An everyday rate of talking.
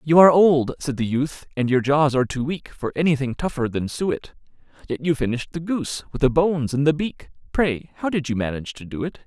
No: fast, 235 wpm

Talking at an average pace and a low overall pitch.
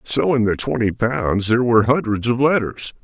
Yes: average, 195 wpm; low, 120 Hz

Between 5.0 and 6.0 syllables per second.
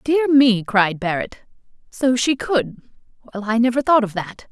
No: 4.5 syllables/s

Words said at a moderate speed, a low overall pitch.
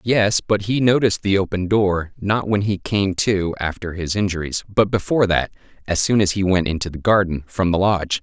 No: fast, 210 wpm; very low, 95 Hz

